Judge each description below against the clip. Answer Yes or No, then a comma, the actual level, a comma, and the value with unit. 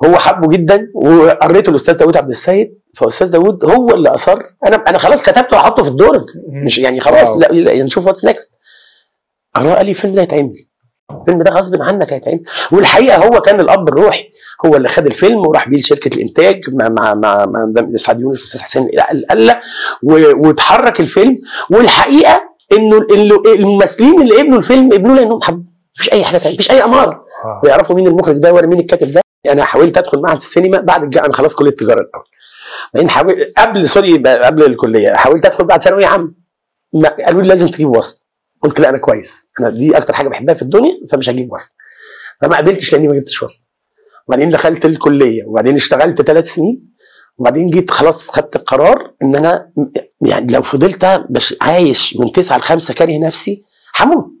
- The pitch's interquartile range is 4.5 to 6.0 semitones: Yes, average, 5.2 semitones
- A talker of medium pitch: Yes, medium, 180 Hz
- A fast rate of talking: Yes, fast, 170 wpm